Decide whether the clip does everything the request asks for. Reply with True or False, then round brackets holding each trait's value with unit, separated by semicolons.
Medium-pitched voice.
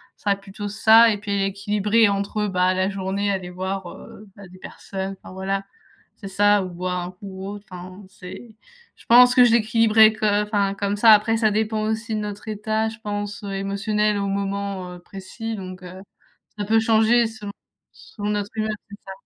False (205 Hz)